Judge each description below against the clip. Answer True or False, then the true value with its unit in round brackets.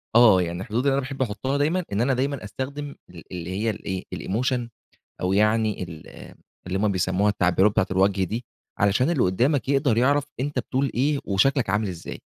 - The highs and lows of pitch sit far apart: True (5.9 semitones)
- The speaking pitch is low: True (110 Hz)